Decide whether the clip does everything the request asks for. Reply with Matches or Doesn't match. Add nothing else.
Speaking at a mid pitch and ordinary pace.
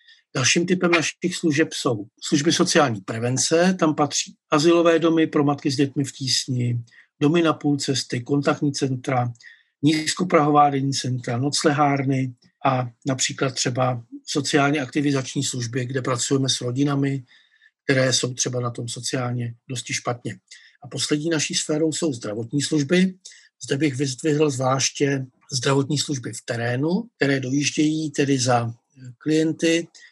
Matches